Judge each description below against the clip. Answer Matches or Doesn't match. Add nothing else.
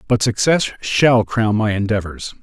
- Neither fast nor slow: Matches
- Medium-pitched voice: Doesn't match